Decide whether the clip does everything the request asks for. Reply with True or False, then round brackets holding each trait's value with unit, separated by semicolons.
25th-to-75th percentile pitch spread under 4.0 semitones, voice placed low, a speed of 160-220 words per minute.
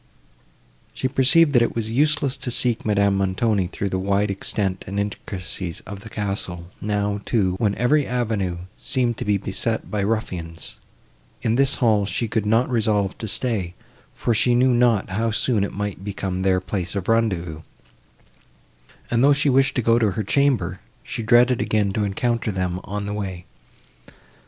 True (3.5 semitones; 105 Hz; 170 wpm)